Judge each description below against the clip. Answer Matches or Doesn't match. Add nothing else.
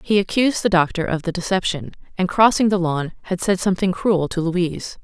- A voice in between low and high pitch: Matches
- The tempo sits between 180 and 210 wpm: Matches